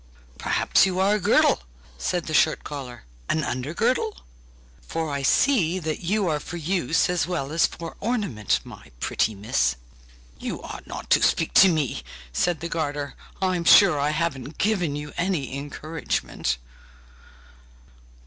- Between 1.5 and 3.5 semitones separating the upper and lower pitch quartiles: No, average, 4.3 semitones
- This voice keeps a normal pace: Yes, average, 150 wpm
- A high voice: No, medium, 160 Hz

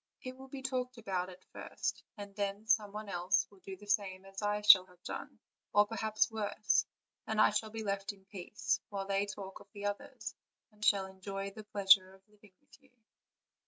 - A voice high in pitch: Yes, high, 205 Hz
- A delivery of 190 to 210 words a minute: Yes, average, 200 wpm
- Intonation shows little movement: Yes, narrow, 1.8 semitones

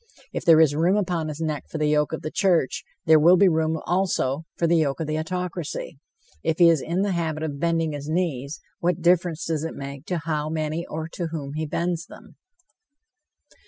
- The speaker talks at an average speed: No, fast, 210 wpm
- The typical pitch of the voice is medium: Yes, medium, 160 Hz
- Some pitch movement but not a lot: No, narrow, 2.0 semitones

